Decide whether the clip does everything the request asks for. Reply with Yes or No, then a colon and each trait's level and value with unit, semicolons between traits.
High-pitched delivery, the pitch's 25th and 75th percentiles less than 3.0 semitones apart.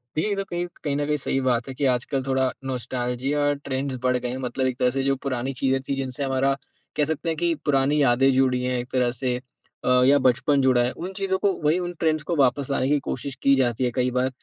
No: low, 135 Hz; narrow, 2.4 semitones